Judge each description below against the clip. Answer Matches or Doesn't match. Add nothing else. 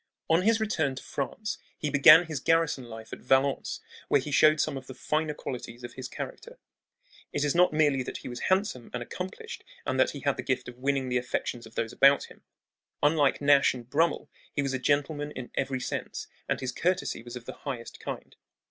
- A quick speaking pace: Matches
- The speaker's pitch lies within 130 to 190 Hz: Matches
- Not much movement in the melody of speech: Doesn't match